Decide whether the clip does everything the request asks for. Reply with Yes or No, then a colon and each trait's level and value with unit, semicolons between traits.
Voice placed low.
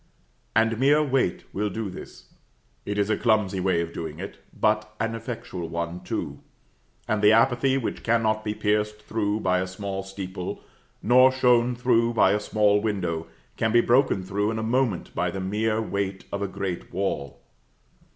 Yes: low, 105 Hz